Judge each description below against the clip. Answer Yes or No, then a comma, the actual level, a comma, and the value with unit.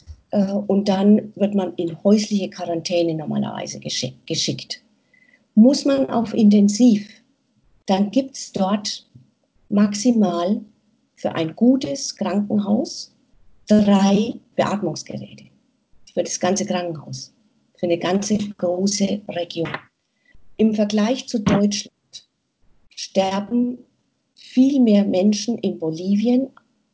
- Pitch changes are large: No, average, 4.5 semitones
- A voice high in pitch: Yes, high, 205 Hz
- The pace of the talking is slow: Yes, slow, 95 wpm